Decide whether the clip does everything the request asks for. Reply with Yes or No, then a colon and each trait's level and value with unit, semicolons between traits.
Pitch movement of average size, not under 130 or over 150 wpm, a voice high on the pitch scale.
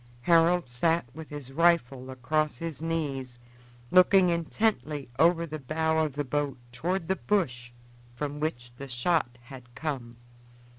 No: average, 4.5 semitones; average, 140 wpm; medium, 150 Hz